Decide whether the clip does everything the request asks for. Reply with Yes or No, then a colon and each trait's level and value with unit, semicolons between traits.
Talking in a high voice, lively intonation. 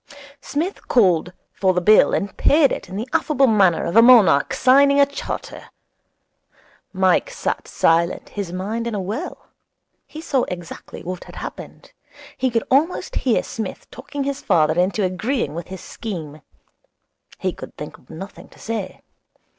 Yes: high, 210 Hz; wide, 6.7 semitones